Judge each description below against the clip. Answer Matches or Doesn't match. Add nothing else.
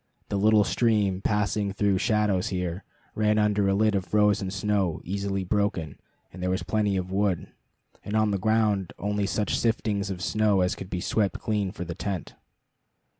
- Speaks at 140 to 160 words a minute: Doesn't match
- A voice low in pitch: Matches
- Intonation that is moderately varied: Doesn't match